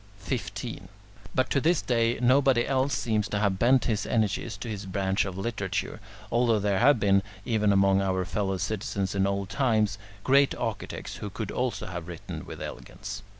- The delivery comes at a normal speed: Yes, average, 175 wpm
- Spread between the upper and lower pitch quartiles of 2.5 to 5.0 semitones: Yes, average, 3.5 semitones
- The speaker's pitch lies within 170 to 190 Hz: No, low, 105 Hz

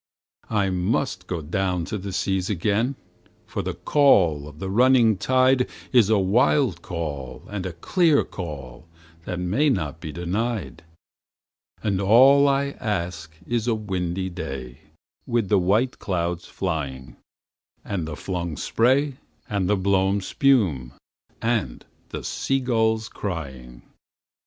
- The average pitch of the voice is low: Yes, very low, 95 Hz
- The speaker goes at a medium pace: No, slow, 130 wpm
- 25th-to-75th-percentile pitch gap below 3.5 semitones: No, wide, 5.4 semitones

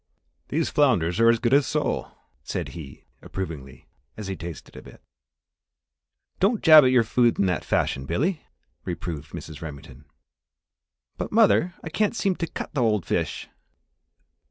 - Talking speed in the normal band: Yes, average, 155 wpm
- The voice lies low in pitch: Yes, low, 115 Hz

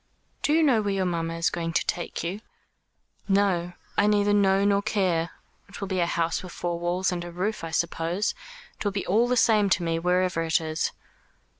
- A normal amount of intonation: Yes, average, 3.1 semitones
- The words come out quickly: Yes, fast, 215 wpm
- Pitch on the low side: No, medium, 185 Hz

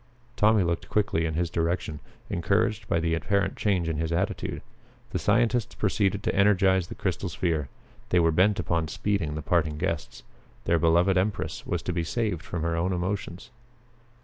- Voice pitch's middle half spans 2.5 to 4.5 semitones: Yes, average, 3.4 semitones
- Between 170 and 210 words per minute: Yes, average, 175 wpm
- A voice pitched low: Yes, very low, 90 Hz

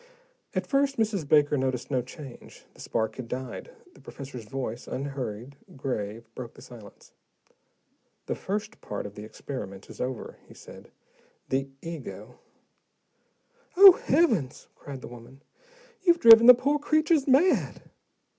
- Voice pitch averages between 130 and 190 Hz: Yes, low, 135 Hz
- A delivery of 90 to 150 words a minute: Yes, average, 140 wpm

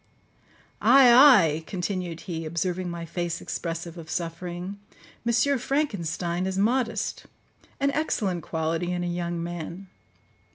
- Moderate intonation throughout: Yes, average, 3.4 semitones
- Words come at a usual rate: No, slow, 120 wpm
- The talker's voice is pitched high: No, medium, 175 Hz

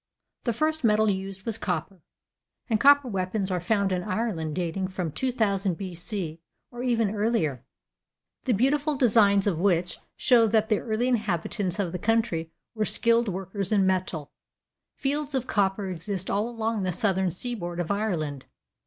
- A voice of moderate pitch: No, high, 200 Hz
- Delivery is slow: No, average, 155 wpm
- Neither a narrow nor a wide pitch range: Yes, average, 4.0 semitones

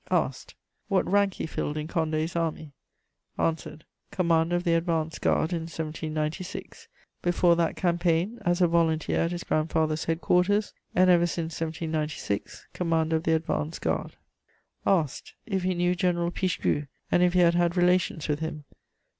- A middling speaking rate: Yes, average, 155 wpm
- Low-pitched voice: No, medium, 165 Hz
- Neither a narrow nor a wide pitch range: No, narrow, 1.8 semitones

